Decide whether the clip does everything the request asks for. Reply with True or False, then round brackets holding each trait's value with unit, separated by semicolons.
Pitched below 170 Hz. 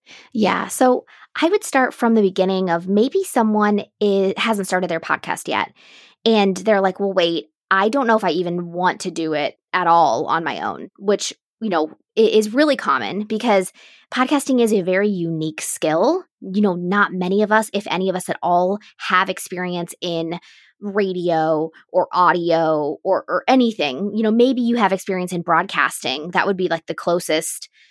False (195 Hz)